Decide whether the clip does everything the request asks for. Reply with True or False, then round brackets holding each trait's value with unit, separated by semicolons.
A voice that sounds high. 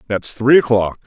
False (115 Hz)